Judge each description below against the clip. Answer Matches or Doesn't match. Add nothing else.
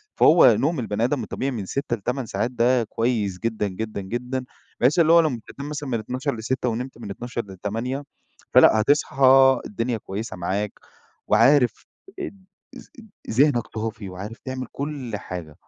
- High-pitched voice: Doesn't match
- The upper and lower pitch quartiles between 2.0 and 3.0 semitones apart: Doesn't match